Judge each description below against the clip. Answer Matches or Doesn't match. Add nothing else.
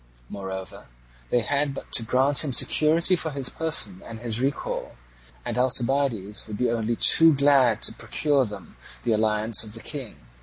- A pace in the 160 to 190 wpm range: Matches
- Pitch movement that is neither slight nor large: Matches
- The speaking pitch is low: Matches